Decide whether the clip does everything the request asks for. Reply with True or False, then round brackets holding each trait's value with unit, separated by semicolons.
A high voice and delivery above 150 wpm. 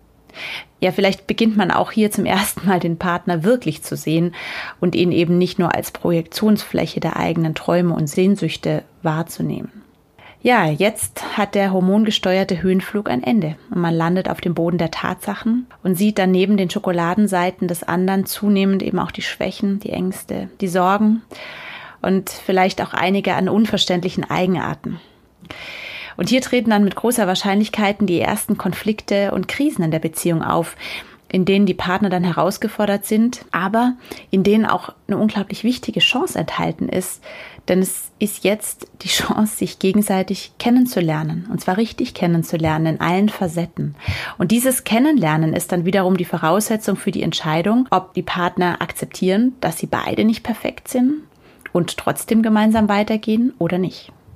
True (195 Hz; 160 wpm)